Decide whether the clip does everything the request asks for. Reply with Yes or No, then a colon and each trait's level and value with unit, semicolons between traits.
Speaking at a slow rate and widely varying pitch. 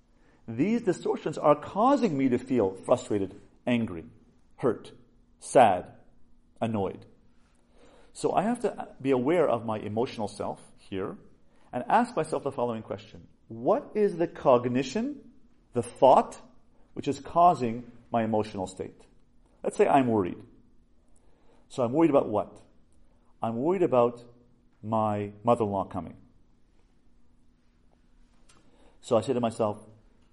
Yes: slow, 125 wpm; wide, 5.9 semitones